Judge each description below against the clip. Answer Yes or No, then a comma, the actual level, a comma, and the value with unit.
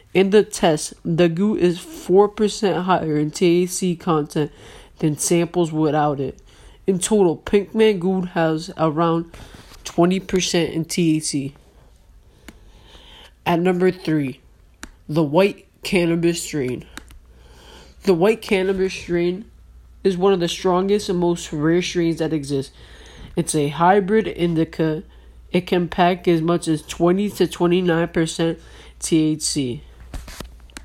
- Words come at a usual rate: No, slow, 120 wpm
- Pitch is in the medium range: Yes, medium, 175 Hz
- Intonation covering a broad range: No, average, 2.8 semitones